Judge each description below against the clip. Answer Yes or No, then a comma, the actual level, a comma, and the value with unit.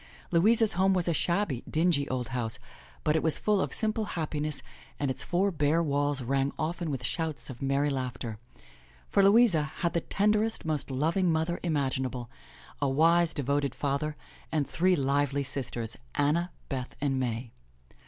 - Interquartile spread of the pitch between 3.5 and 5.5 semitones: Yes, average, 4.1 semitones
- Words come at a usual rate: Yes, average, 165 wpm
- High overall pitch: No, medium, 150 Hz